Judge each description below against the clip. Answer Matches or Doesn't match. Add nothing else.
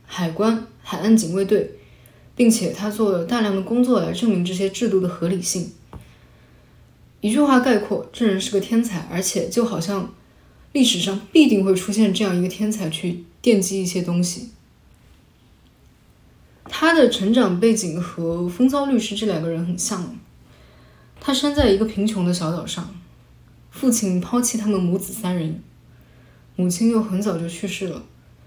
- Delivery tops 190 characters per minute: Matches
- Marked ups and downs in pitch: Doesn't match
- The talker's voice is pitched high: Matches